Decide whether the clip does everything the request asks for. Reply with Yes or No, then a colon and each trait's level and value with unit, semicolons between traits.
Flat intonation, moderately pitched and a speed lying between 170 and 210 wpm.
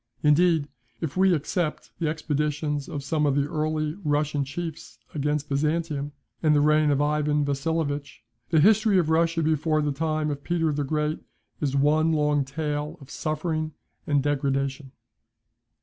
No: narrow, 1.6 semitones; medium, 150 Hz; average, 150 wpm